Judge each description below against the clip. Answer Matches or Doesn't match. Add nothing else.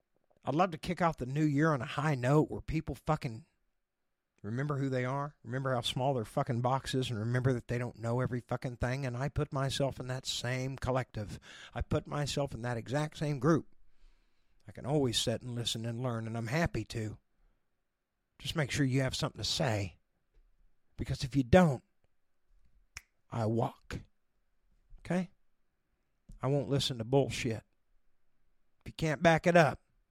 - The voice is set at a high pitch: Doesn't match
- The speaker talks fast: Doesn't match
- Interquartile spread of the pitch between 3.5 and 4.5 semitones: Matches